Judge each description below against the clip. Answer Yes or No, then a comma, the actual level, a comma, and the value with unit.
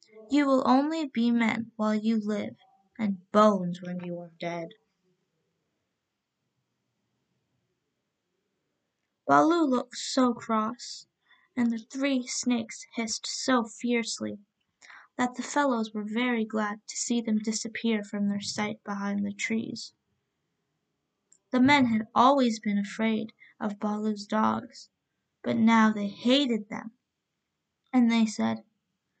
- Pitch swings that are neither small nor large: Yes, average, 3.0 semitones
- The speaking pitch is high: Yes, high, 225 Hz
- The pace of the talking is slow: Yes, slow, 120 wpm